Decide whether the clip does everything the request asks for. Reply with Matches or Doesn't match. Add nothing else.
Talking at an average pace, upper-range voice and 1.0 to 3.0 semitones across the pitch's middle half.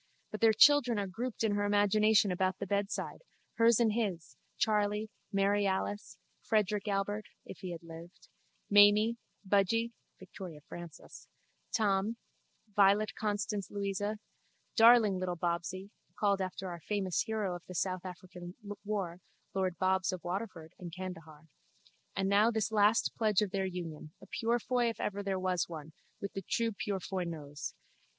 Matches